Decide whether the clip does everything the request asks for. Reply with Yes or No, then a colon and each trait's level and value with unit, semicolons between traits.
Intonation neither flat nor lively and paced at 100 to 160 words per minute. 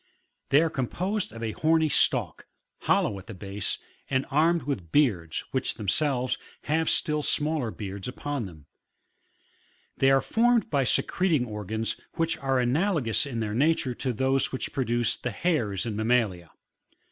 No: wide, 5.7 semitones; average, 155 wpm